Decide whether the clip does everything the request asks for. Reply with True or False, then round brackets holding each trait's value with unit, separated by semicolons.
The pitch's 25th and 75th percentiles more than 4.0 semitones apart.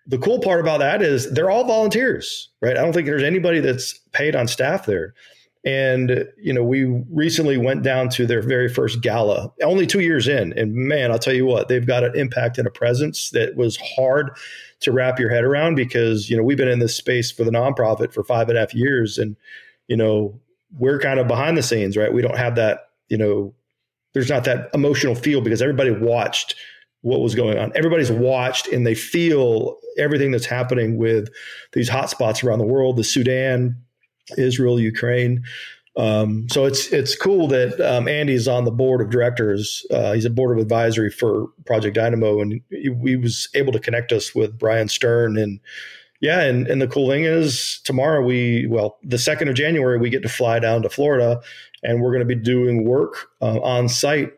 False (2.6 semitones)